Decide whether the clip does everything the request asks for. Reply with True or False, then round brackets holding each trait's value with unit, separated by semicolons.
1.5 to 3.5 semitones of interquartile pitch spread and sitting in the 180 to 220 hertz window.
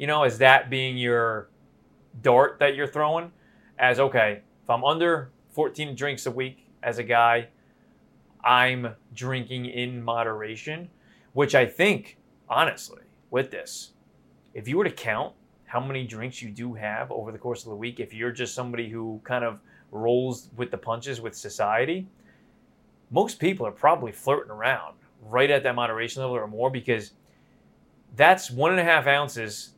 False (2.7 semitones; 125 Hz)